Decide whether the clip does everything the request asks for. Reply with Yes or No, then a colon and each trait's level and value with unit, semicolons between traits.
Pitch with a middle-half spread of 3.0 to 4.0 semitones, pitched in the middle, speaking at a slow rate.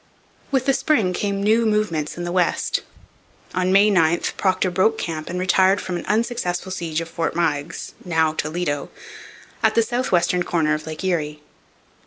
No: average, 3.6 semitones; medium, 180 Hz; average, 170 wpm